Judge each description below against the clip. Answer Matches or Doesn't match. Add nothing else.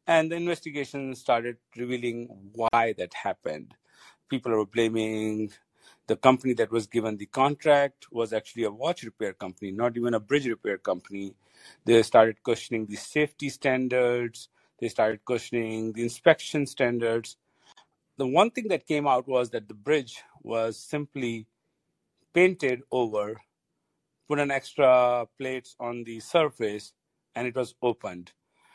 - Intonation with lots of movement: Doesn't match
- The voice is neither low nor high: Doesn't match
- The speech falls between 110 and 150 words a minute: Matches